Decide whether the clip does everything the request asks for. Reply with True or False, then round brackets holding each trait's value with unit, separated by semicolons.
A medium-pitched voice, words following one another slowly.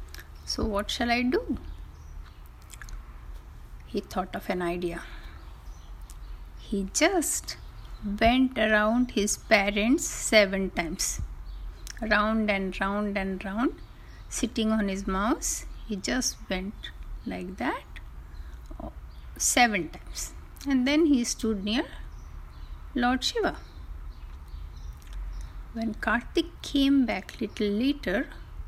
False (195 Hz; 100 wpm)